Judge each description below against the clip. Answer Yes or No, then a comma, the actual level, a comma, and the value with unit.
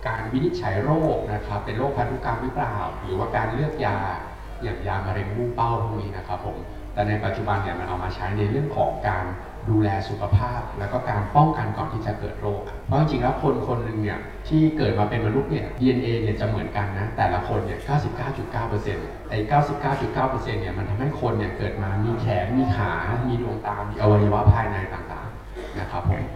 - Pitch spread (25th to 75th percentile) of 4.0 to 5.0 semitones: No, average, 3.3 semitones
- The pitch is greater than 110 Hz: No, low, 105 Hz